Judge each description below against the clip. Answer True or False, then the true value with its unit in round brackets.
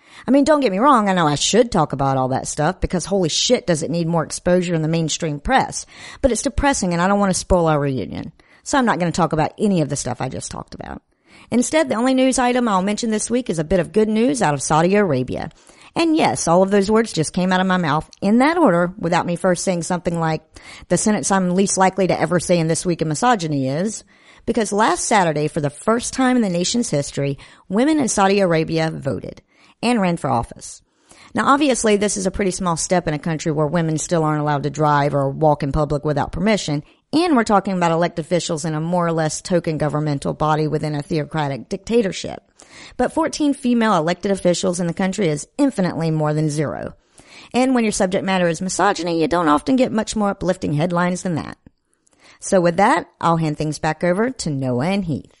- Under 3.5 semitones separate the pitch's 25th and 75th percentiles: False (5.5 semitones)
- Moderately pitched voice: True (180 Hz)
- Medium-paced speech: False (230 wpm)